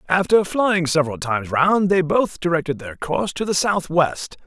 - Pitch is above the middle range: No, medium, 170 Hz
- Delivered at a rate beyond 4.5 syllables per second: Yes, 5.0 syllables/s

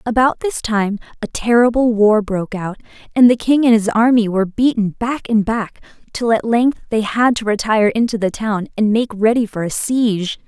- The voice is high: Yes, high, 220 Hz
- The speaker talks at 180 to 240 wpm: Yes, average, 200 wpm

